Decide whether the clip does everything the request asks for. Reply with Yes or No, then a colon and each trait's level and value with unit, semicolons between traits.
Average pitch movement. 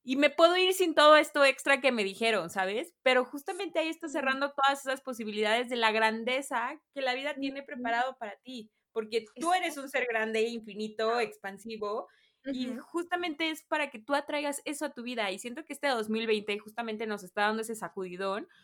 Yes: average, 4.8 semitones